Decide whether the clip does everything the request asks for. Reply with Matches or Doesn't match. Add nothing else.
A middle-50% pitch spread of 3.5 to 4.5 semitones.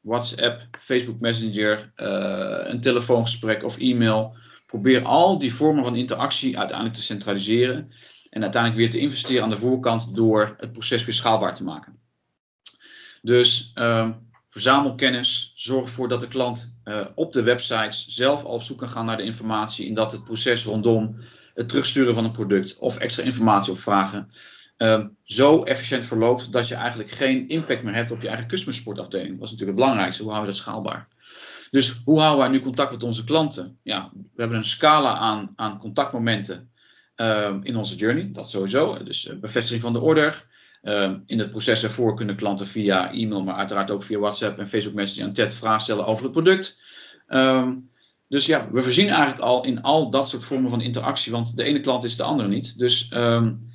Doesn't match